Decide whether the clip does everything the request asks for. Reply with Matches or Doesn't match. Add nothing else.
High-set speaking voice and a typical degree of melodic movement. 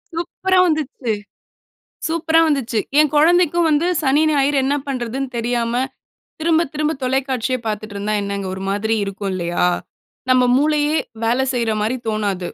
Doesn't match